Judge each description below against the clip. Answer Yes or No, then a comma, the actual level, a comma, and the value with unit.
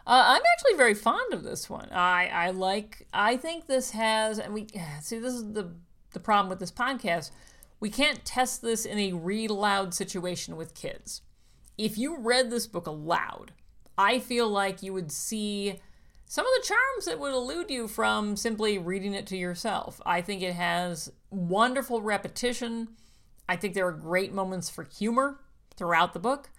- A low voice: No, high, 205 Hz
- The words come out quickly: No, average, 180 wpm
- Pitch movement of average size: Yes, average, 4.8 semitones